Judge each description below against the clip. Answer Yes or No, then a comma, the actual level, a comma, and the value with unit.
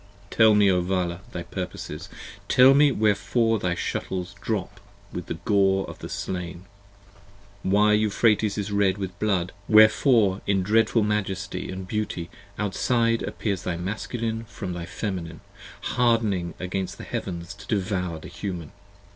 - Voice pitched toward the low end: Yes, low, 100 Hz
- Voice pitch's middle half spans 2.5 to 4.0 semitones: Yes, average, 2.9 semitones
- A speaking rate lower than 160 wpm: Yes, average, 145 wpm